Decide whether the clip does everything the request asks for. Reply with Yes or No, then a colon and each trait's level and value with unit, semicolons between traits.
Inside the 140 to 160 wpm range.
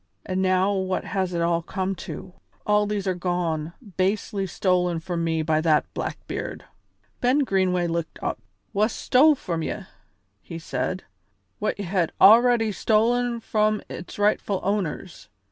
Yes: average, 145 wpm